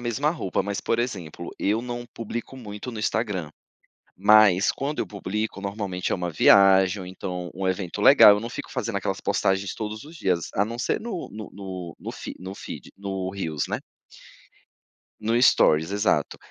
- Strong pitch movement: No, average, 3.4 semitones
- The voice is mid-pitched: No, low, 100 Hz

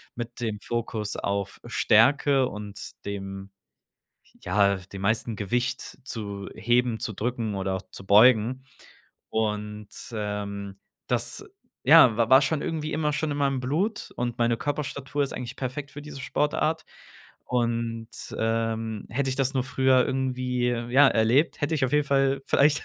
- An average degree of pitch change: Yes, average, 4.2 semitones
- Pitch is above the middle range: No, low, 120 Hz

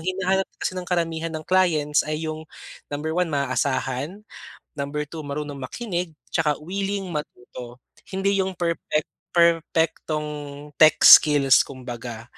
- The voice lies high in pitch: No, medium, 155 Hz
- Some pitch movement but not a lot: Yes, average, 3.8 semitones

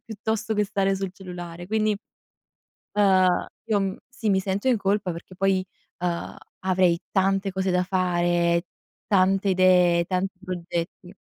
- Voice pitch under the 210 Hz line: Yes, high, 190 Hz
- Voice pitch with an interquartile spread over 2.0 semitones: No, narrow, 1.7 semitones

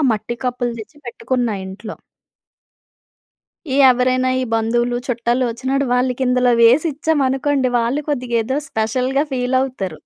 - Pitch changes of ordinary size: No, narrow, 1.9 semitones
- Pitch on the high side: Yes, very high, 250 Hz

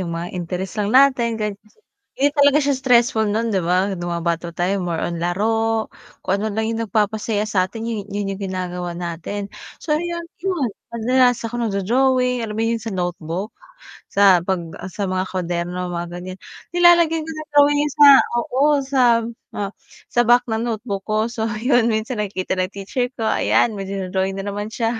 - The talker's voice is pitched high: Yes, high, 215 Hz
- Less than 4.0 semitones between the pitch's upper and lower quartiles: No, average, 4.6 semitones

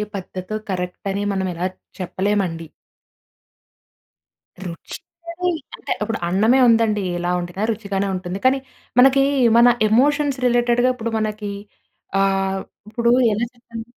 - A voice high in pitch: Yes, high, 210 Hz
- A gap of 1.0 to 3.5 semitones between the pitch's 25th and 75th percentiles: No, average, 4.0 semitones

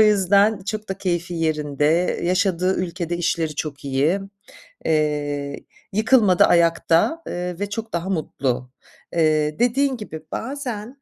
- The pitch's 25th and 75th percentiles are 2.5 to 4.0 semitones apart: No, average, 4.9 semitones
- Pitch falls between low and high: Yes, medium, 175 Hz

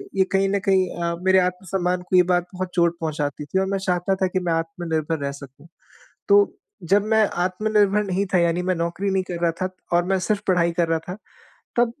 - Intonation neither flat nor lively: No, narrow, 2.2 semitones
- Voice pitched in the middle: Yes, medium, 180 Hz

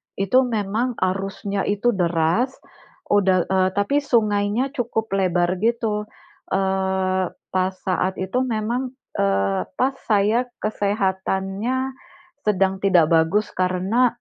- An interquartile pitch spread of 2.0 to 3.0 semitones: No, average, 3.4 semitones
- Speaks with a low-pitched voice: No, high, 200 Hz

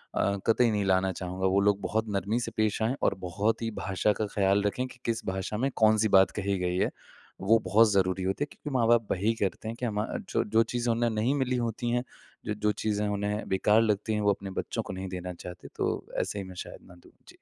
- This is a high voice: No, low, 105 Hz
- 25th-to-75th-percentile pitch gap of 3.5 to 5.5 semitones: No, average, 2.9 semitones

